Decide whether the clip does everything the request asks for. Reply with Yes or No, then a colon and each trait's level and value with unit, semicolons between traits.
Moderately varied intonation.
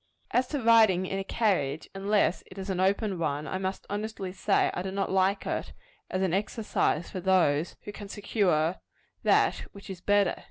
No: narrow, 2.0 semitones